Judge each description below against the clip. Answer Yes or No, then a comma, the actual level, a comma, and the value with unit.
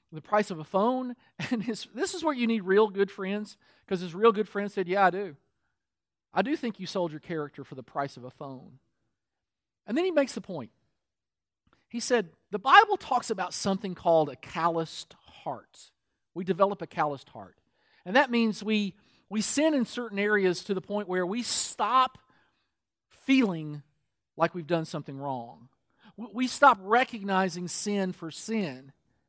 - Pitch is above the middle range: Yes, high, 195 Hz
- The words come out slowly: No, average, 175 wpm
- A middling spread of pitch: No, wide, 6.4 semitones